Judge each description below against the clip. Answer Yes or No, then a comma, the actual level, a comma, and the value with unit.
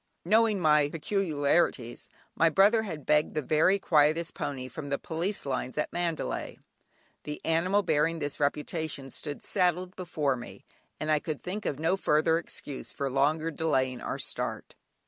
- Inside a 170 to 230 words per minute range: No, average, 155 wpm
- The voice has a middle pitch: Yes, medium, 155 Hz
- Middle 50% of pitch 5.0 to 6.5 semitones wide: No, average, 3.3 semitones